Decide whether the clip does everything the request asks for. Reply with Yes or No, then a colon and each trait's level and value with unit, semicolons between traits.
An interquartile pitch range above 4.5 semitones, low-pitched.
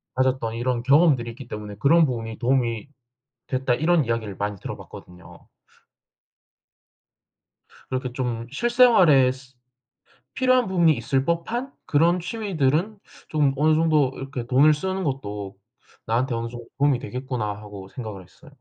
Yes: average, 5.2 semitones; low, 130 Hz